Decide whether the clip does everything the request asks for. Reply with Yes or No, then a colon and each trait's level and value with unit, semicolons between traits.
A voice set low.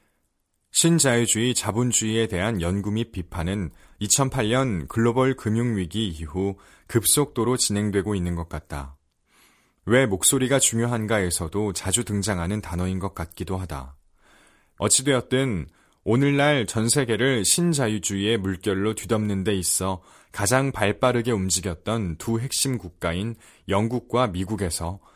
Yes: low, 105 Hz